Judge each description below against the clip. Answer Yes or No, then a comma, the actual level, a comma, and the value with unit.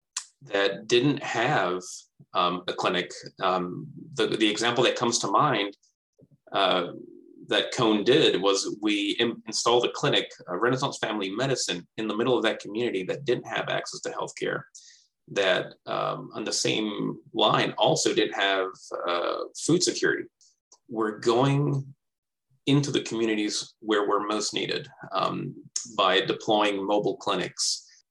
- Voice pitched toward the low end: Yes, low, 130 Hz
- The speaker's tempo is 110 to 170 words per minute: Yes, average, 140 wpm